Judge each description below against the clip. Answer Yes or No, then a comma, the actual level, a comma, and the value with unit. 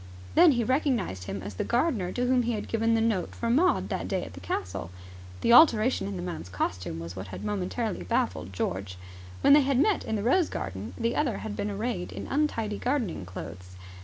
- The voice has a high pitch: Yes, high, 210 Hz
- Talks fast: Yes, fast, 215 wpm